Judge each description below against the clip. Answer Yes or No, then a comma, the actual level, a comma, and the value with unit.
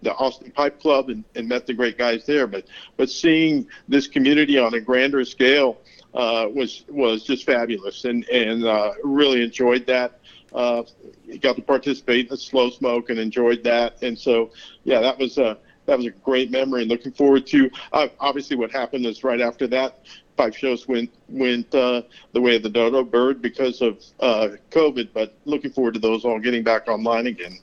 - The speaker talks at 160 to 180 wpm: No, average, 195 wpm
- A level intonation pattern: Yes, narrow, 2.2 semitones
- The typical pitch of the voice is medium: No, low, 125 Hz